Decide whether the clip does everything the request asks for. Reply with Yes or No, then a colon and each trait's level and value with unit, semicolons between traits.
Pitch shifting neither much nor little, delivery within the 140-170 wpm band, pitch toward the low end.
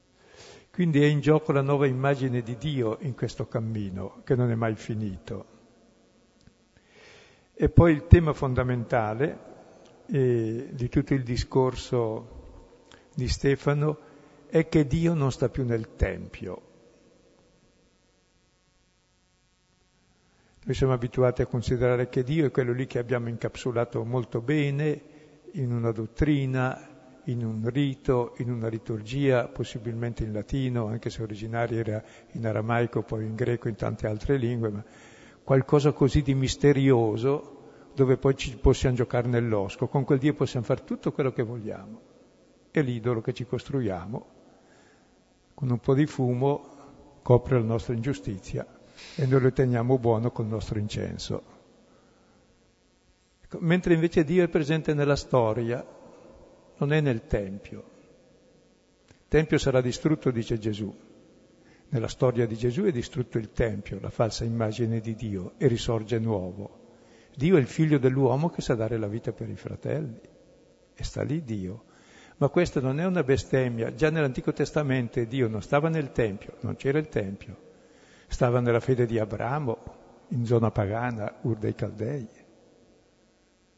Yes: average, 3.8 semitones; average, 145 wpm; low, 125 Hz